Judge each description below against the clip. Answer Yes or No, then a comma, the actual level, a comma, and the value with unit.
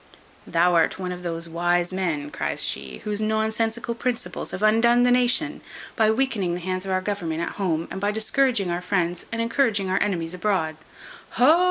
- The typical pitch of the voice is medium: No, high, 195 Hz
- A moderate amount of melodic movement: Yes, average, 4.5 semitones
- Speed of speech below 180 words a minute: No, average, 185 wpm